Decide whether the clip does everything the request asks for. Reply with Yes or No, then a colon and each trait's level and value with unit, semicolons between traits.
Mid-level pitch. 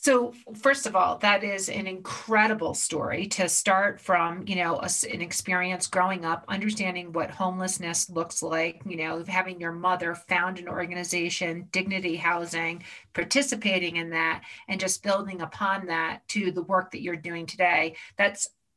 Yes: medium, 180 Hz